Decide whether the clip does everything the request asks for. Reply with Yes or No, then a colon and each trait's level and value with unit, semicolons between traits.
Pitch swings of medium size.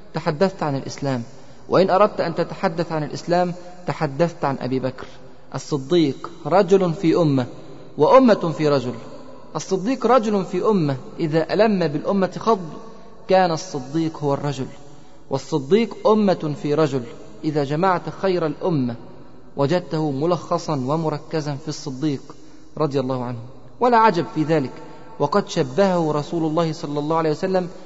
Yes: average, 4.0 semitones